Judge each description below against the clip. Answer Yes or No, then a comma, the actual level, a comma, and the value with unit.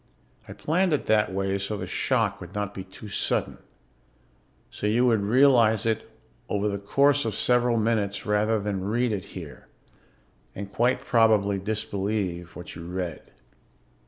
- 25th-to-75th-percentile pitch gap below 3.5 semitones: Yes, average, 2.7 semitones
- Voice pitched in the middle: No, low, 105 Hz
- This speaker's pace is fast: No, average, 155 wpm